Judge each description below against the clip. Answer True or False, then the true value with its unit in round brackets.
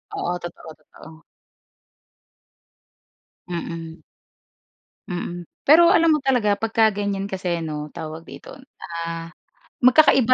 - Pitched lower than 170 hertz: False (180 Hz)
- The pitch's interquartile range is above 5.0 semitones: True (5.4 semitones)